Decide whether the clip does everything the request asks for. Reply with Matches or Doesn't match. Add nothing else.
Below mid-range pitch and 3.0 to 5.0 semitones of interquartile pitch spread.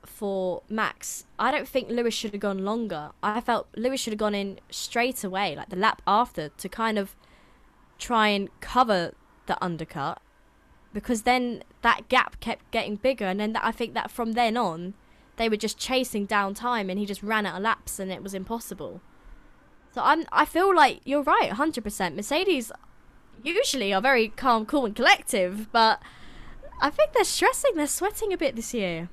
Doesn't match